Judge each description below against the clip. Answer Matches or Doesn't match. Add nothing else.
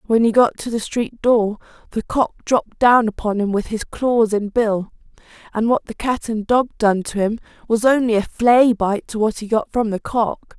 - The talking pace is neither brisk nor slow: Doesn't match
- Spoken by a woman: Matches